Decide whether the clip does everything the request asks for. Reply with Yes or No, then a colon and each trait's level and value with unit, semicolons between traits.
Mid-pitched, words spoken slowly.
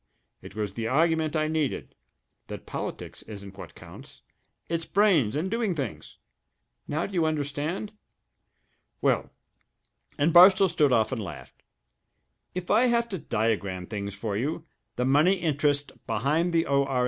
No: medium, 150 Hz; average, 145 wpm